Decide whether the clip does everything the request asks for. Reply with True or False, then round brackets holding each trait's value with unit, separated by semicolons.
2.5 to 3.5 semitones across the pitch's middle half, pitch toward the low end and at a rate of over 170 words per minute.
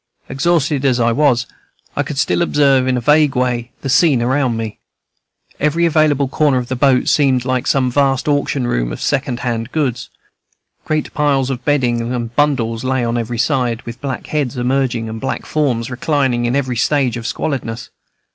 True (3.1 semitones; 130 Hz; 180 wpm)